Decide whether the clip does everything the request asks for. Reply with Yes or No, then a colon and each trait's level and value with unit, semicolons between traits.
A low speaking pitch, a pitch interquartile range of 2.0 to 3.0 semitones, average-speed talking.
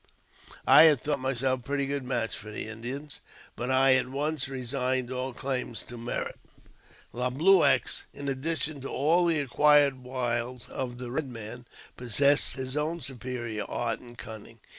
Yes: low, 130 Hz; average, 2.7 semitones; average, 160 wpm